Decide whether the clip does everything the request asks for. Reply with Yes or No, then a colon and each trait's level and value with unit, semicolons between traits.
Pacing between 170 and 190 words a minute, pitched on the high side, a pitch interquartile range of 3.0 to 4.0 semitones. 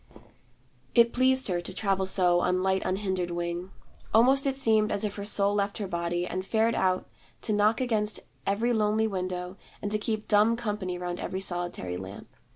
Yes: average, 180 wpm; high, 200 Hz; average, 3.3 semitones